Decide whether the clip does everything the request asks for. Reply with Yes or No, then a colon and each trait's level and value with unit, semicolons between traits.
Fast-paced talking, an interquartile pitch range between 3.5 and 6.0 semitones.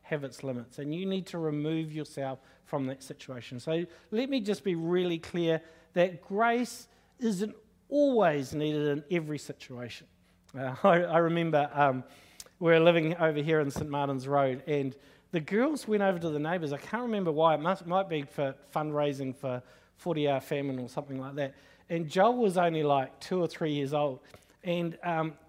No: average, 185 wpm; average, 3.8 semitones